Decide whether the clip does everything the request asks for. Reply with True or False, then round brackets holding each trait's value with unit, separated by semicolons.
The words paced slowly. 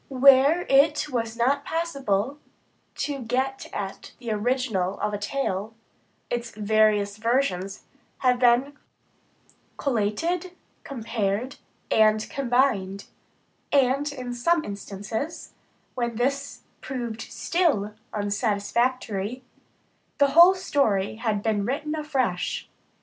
True (100 wpm)